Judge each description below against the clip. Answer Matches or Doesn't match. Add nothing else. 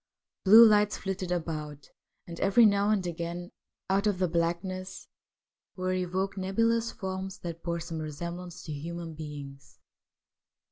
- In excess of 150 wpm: Doesn't match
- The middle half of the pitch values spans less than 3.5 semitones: Matches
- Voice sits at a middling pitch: Matches